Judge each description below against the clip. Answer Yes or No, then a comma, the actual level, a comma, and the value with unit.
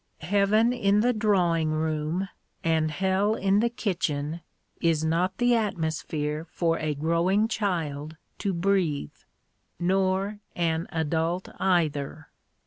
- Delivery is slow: Yes, slow, 115 wpm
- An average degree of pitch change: Yes, average, 3.9 semitones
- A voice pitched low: No, medium, 170 Hz